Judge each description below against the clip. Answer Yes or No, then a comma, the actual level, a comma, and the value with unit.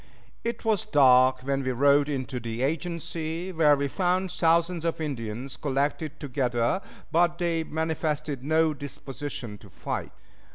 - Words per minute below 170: Yes, slow, 135 wpm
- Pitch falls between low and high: Yes, medium, 150 Hz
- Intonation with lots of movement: No, average, 4.0 semitones